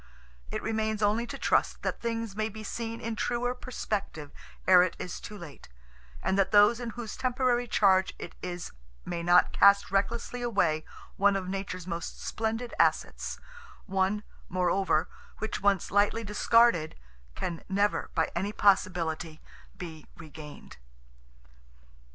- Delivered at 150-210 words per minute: No, average, 140 wpm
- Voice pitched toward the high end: Yes, high, 200 Hz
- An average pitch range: Yes, average, 3.9 semitones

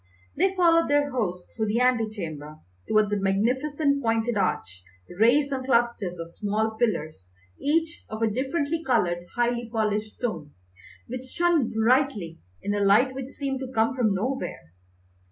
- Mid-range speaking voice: No, high, 235 Hz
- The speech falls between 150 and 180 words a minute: Yes, average, 155 wpm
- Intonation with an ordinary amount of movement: Yes, average, 4.7 semitones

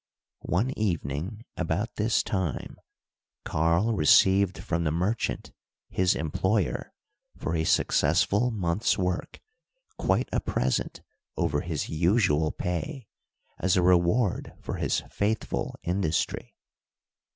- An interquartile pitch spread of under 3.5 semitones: No, average, 4.1 semitones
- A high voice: No, very low, 90 Hz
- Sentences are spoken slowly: Yes, slow, 105 wpm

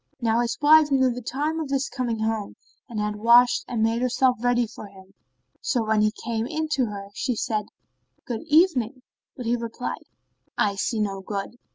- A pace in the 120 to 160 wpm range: No, average, 190 wpm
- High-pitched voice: Yes, high, 235 Hz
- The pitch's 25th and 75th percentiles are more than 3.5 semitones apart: No, average, 3.1 semitones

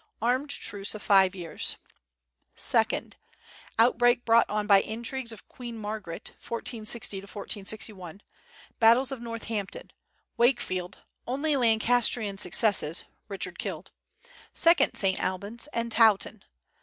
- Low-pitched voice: No, high, 220 Hz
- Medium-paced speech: No, slow, 105 wpm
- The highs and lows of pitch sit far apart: No, average, 3.2 semitones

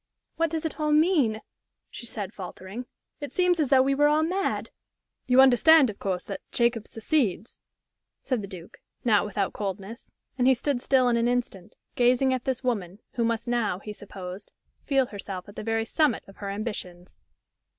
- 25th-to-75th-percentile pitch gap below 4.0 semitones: No, average, 4.9 semitones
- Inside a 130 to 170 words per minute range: No, average, 180 wpm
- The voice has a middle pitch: No, high, 235 Hz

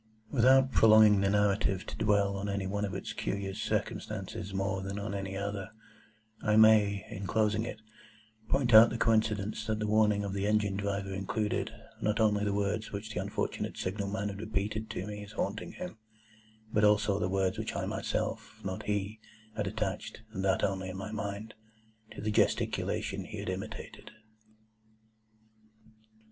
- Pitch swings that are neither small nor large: No, narrow, 1.7 semitones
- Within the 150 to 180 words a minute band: Yes, average, 165 wpm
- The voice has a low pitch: Yes, low, 105 Hz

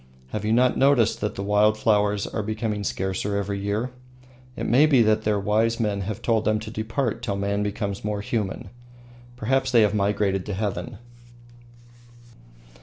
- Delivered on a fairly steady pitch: Yes, narrow, 2.0 semitones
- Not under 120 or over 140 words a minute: No, average, 170 wpm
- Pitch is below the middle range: Yes, low, 105 Hz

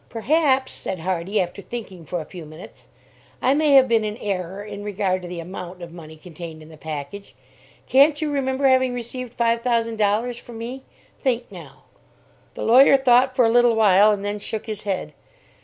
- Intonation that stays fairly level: No, average, 5.3 semitones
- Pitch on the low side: No, high, 215 Hz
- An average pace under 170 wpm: No, average, 190 wpm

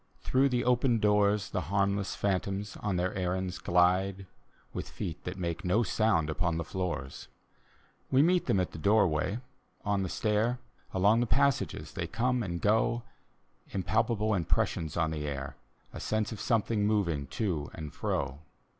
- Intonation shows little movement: No, average, 4.0 semitones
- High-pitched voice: No, low, 100 Hz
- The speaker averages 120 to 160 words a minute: Yes, average, 155 wpm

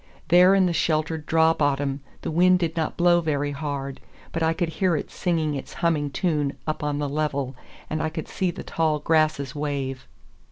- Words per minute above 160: Yes, average, 195 wpm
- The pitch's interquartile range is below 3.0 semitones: Yes, narrow, 2.5 semitones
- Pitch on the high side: No, medium, 155 Hz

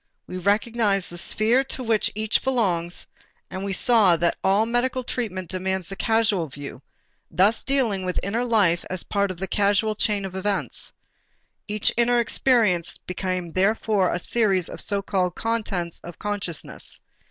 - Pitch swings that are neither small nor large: Yes, average, 3.5 semitones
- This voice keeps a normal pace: Yes, average, 155 wpm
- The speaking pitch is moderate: No, high, 200 Hz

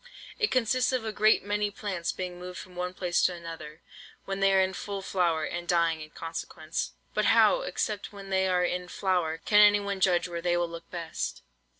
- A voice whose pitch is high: No, medium, 180 Hz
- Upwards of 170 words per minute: Yes, fast, 205 wpm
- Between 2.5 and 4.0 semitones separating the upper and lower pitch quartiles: Yes, average, 2.8 semitones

